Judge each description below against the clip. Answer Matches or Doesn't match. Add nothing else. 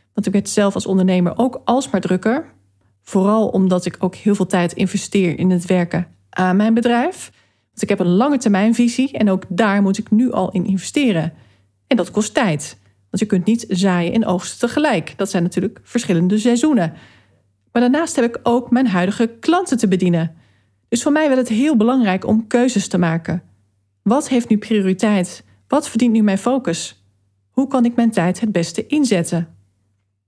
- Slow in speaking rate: Doesn't match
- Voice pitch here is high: Matches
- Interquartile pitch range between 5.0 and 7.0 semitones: Matches